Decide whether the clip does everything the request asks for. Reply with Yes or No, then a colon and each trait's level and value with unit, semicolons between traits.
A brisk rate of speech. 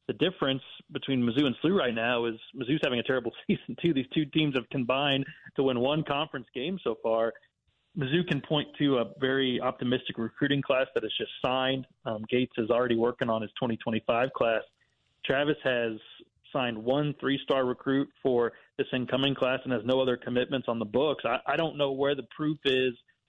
No: average, 195 wpm